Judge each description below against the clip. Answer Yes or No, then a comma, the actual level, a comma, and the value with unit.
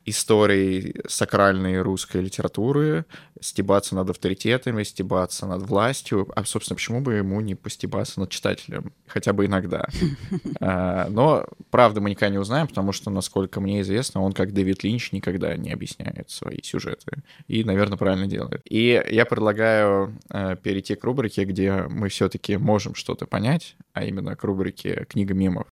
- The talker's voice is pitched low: Yes, low, 100 Hz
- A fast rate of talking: No, average, 150 wpm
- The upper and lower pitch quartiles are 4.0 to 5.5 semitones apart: No, average, 3.2 semitones